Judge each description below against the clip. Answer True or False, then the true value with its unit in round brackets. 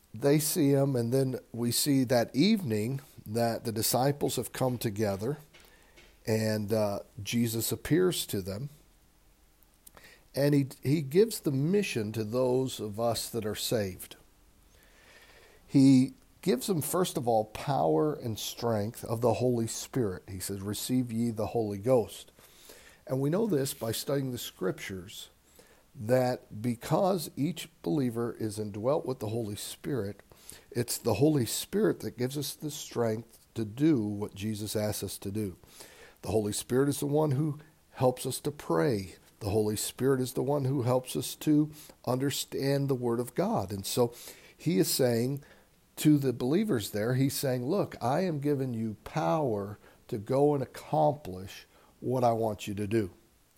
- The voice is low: True (125 Hz)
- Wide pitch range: False (4.5 semitones)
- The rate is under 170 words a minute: True (160 wpm)